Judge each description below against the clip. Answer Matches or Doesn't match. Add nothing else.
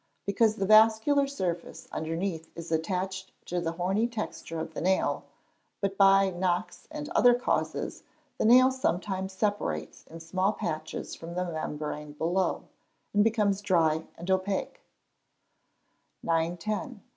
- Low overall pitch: Doesn't match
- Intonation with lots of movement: Doesn't match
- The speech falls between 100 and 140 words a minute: Matches